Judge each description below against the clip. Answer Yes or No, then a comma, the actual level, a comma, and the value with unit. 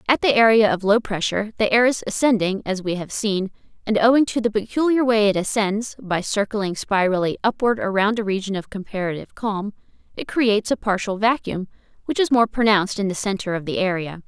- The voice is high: Yes, high, 210 Hz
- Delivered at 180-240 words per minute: Yes, average, 190 wpm